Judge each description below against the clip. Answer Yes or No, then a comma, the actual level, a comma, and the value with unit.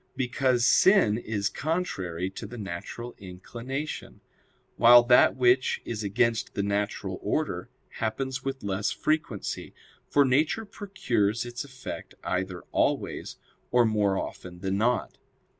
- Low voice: Yes, low, 120 Hz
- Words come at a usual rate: No, slow, 125 wpm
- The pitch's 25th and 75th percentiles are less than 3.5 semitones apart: No, average, 4.6 semitones